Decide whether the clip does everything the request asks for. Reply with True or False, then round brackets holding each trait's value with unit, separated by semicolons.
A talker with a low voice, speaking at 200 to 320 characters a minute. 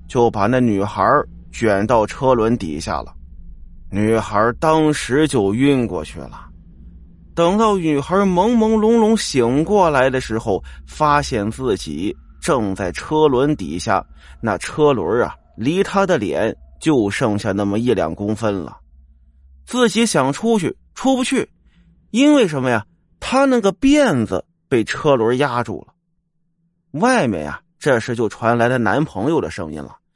True (125 Hz; 205 characters per minute)